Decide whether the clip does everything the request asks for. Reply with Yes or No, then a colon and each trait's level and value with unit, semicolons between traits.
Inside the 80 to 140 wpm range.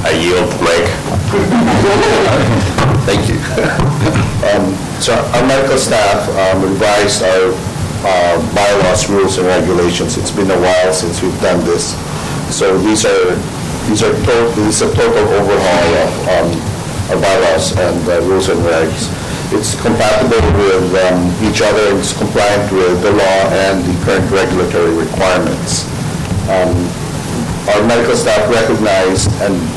Yes: slow, 135 wpm